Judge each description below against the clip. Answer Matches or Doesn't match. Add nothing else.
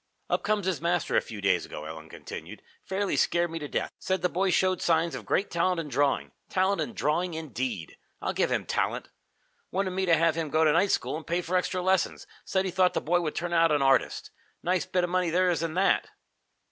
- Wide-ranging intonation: Doesn't match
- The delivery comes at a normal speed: Doesn't match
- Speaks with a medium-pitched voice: Matches